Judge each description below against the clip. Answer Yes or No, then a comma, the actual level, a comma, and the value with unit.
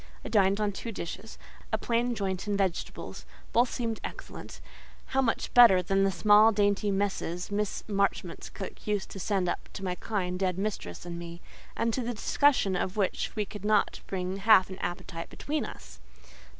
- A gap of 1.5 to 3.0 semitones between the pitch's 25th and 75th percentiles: Yes, narrow, 2.6 semitones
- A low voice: No, high, 200 Hz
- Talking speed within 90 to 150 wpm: No, average, 175 wpm